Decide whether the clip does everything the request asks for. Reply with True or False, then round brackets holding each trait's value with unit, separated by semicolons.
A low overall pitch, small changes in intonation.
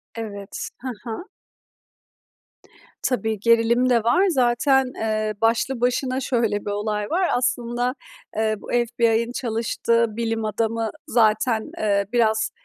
False (230 Hz; 2.0 semitones)